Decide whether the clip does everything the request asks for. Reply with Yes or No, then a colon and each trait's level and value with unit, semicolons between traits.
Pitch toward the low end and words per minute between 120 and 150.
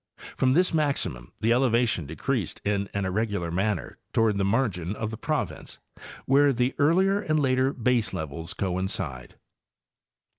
Yes: low, 110 Hz; average, 140 wpm